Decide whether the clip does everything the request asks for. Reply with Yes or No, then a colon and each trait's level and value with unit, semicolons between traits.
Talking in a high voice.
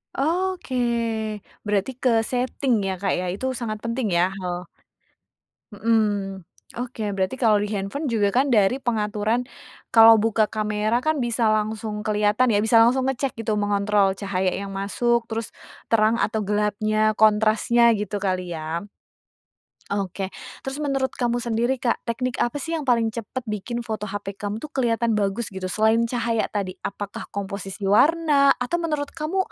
Yes: high, 220 Hz